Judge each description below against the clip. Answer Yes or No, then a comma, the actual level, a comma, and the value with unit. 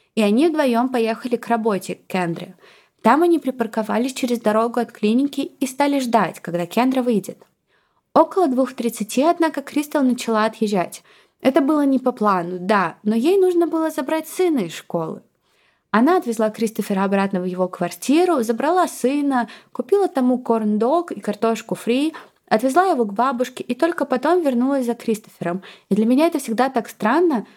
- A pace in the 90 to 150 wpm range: No, fast, 160 wpm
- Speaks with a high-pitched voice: Yes, high, 240 Hz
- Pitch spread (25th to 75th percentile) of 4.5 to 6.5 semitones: Yes, average, 5.1 semitones